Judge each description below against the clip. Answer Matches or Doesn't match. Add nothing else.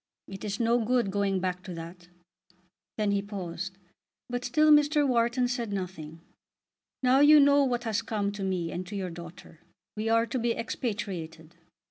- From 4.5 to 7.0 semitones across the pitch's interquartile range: Matches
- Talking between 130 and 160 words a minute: Doesn't match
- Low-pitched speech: Doesn't match